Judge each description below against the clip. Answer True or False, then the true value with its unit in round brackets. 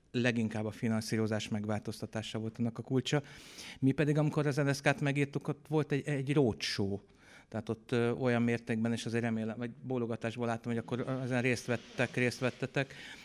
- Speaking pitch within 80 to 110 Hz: False (120 Hz)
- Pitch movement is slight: False (3.6 semitones)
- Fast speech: True (170 wpm)